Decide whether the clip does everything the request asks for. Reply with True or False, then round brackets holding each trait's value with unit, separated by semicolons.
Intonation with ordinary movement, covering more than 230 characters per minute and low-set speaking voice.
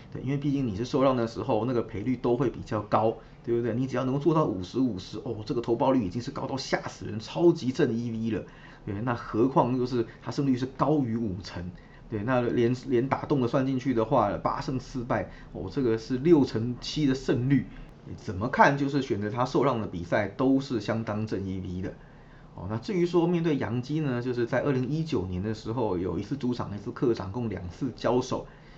True (3.8 semitones; 315 characters per minute; 125 Hz)